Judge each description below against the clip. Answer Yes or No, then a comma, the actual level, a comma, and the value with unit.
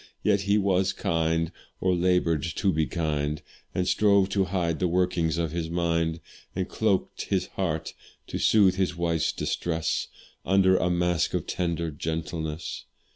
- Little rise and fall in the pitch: Yes, narrow, 2.3 semitones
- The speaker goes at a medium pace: Yes, average, 150 wpm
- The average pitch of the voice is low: Yes, very low, 85 Hz